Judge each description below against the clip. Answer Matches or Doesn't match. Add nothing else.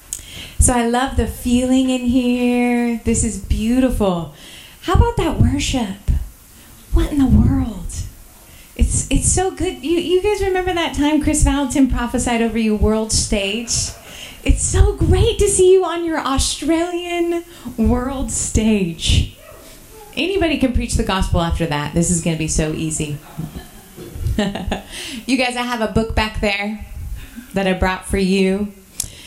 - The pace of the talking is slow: Doesn't match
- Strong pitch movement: Matches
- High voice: Matches